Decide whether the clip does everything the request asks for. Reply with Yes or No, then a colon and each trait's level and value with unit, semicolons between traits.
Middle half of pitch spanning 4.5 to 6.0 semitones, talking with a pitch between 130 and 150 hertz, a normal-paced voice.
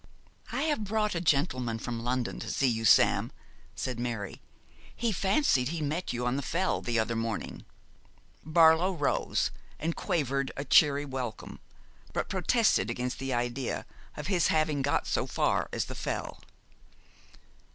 Yes: wide, 5.4 semitones; medium, 140 Hz; average, 150 wpm